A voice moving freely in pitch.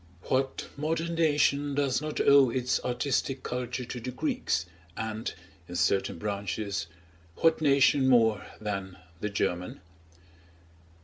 No: average, 5.0 semitones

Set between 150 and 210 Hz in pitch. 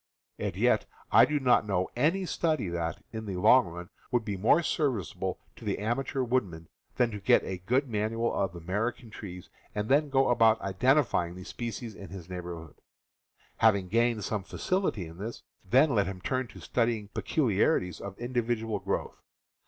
No: low, 110 Hz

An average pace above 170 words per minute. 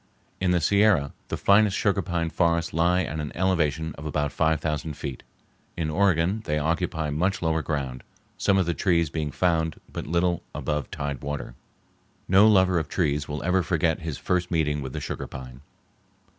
Yes: average, 180 wpm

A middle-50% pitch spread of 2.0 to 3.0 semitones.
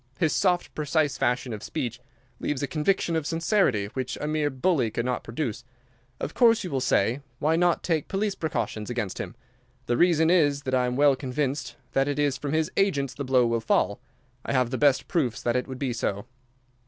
No: average, 4.3 semitones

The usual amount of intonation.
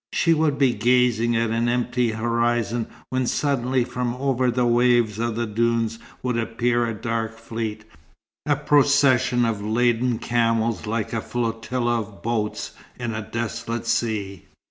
No: narrow, 1.5 semitones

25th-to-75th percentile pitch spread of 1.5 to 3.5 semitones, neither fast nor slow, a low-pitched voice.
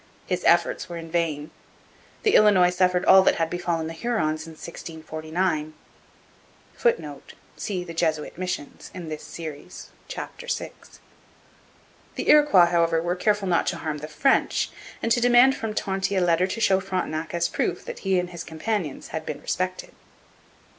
No: average, 3.1 semitones; average, 160 wpm; medium, 175 Hz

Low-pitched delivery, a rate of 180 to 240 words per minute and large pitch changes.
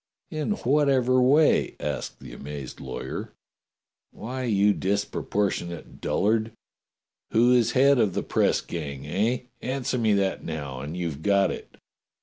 No: low, 105 Hz; slow, 135 wpm; wide, 6.8 semitones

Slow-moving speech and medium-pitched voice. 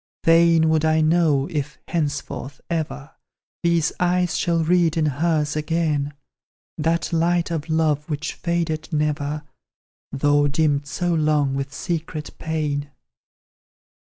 Yes: slow, 120 wpm; medium, 155 Hz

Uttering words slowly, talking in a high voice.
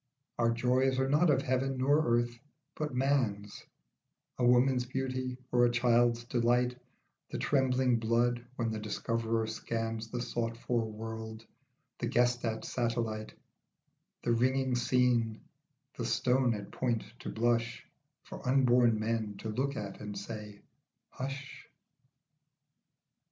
No: slow, 130 wpm; low, 120 Hz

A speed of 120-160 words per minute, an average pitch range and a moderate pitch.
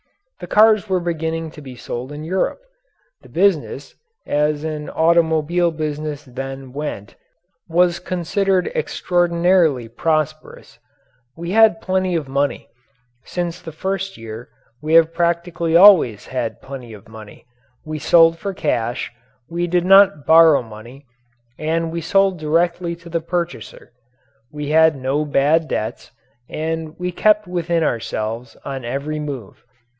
Yes: slow, 135 wpm; average, 3.7 semitones; medium, 160 Hz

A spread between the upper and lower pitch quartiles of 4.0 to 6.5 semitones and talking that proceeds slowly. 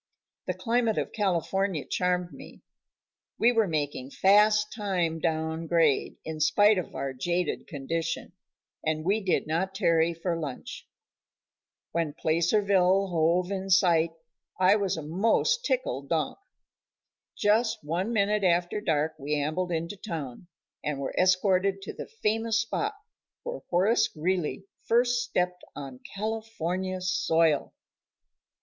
Yes: average, 4.3 semitones; slow, 130 wpm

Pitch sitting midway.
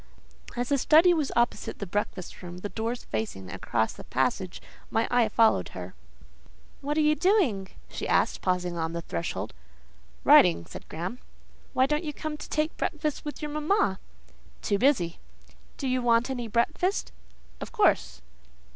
No: high, 235 Hz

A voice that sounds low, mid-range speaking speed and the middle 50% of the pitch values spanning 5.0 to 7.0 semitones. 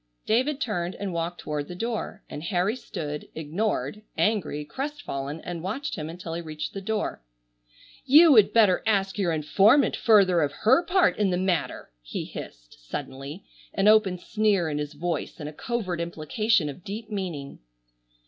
No: medium, 185 Hz; average, 165 wpm; wide, 5.6 semitones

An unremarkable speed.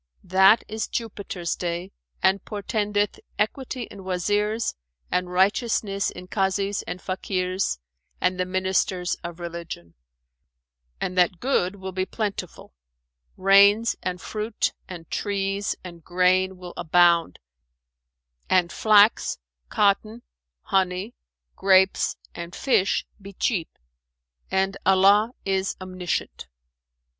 No: slow, 105 wpm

